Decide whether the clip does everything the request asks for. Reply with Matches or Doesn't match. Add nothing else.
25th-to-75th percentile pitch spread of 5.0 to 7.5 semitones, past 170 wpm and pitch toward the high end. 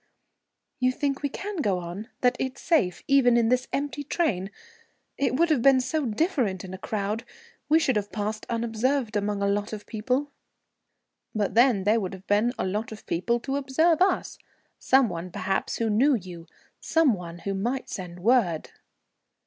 Matches